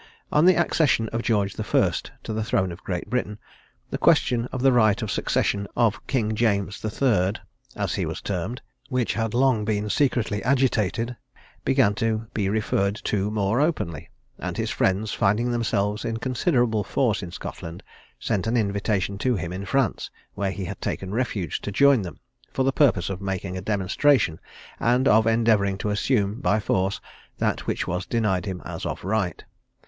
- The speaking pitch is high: No, low, 105 Hz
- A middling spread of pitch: Yes, average, 3.4 semitones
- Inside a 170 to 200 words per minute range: Yes, average, 180 wpm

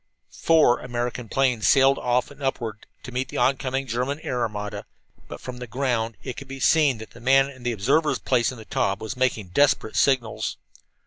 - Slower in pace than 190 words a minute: No, average, 195 wpm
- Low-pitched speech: Yes, low, 125 Hz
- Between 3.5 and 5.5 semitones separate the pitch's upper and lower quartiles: No, average, 2.9 semitones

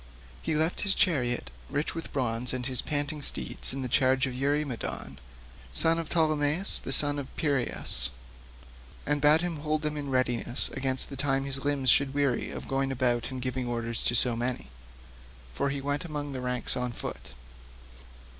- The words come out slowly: No, average, 175 wpm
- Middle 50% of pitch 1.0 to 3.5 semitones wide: Yes, average, 2.7 semitones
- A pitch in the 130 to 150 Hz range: Yes, low, 135 Hz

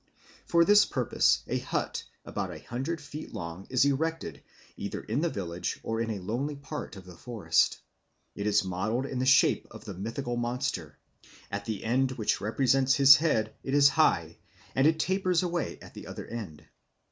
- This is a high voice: No, low, 125 Hz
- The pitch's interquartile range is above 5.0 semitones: Yes, wide, 5.4 semitones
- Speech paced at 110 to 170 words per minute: No, average, 180 wpm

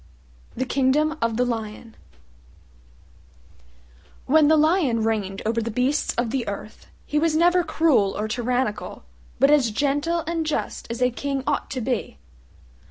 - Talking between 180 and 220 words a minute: No, average, 150 wpm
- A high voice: Yes, very high, 260 Hz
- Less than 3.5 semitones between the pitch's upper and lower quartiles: No, average, 5.1 semitones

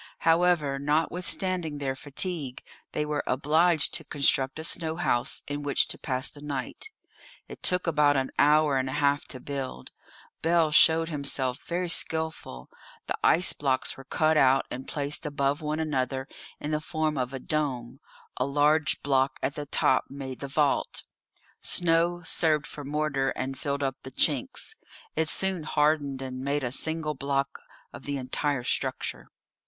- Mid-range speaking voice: Yes, medium, 145 Hz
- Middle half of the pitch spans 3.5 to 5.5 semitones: No, average, 2.8 semitones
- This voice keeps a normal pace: Yes, average, 160 wpm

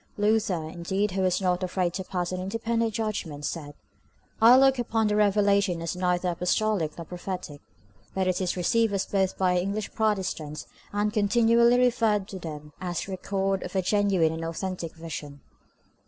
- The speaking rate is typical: Yes, average, 175 wpm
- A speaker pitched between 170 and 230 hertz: Yes, high, 190 Hz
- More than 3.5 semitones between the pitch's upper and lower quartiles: No, average, 3.2 semitones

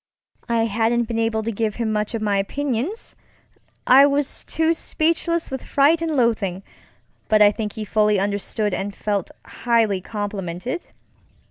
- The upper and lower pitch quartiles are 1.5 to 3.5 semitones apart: No, average, 4.3 semitones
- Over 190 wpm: No, average, 140 wpm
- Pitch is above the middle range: Yes, high, 225 Hz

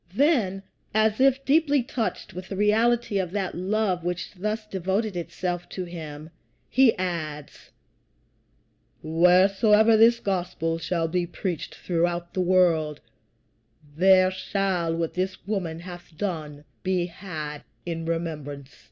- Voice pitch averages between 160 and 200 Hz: Yes, medium, 185 Hz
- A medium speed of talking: No, slow, 125 wpm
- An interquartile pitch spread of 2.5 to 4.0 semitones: Yes, average, 3.7 semitones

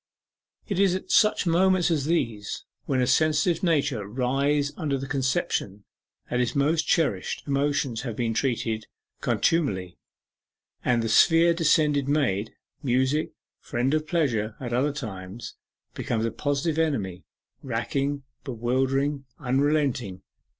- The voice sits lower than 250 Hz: Yes, low, 135 Hz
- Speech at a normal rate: No, slow, 130 wpm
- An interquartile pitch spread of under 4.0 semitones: No, average, 4.5 semitones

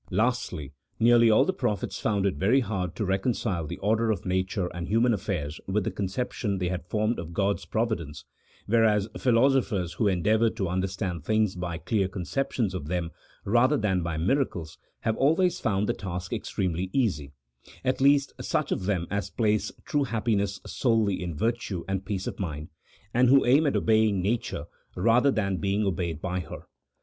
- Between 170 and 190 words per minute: Yes, average, 180 wpm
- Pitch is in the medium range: No, low, 100 Hz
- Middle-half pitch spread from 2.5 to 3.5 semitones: No, average, 4.1 semitones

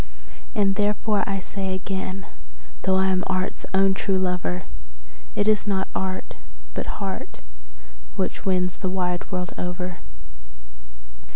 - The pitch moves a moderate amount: No, narrow, 1.2 semitones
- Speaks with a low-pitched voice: No, high, 190 Hz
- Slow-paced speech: Yes, slow, 130 wpm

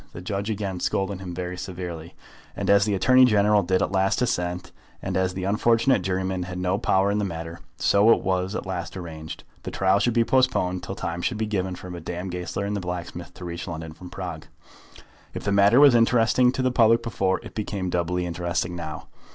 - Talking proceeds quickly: Yes, fast, 210 wpm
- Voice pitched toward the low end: Yes, very low, 95 Hz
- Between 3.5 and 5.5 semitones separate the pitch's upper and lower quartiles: No, average, 2.8 semitones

